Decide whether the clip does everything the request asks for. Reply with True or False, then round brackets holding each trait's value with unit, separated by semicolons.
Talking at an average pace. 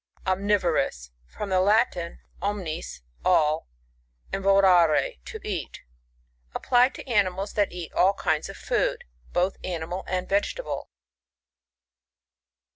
False (115 wpm)